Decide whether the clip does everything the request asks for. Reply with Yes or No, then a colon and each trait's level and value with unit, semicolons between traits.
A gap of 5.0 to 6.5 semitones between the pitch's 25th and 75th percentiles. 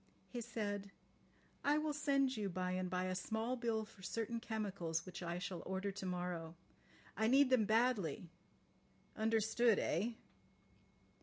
No: average, 4.3 semitones